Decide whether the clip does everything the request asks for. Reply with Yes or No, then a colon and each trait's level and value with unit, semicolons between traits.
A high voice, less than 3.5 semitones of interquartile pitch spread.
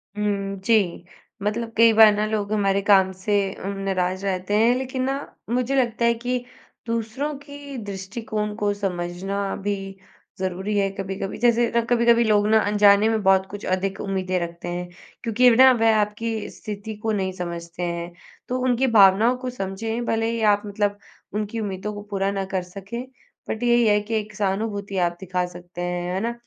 Yes: high, 205 Hz; average, 3.0 semitones